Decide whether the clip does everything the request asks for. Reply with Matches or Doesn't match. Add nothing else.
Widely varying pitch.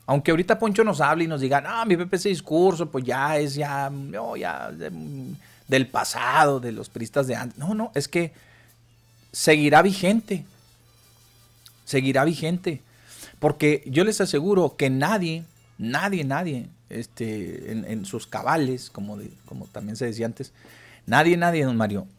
Matches